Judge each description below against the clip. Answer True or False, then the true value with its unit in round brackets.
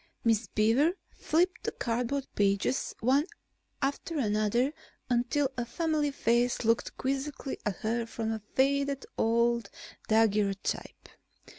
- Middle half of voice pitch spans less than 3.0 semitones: False (3.9 semitones)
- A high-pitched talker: True (240 Hz)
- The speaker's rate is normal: False (115 wpm)